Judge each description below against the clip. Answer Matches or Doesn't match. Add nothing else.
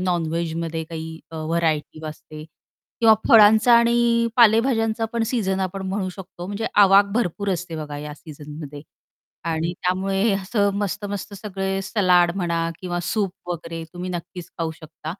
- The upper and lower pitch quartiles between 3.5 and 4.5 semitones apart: Matches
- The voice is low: Doesn't match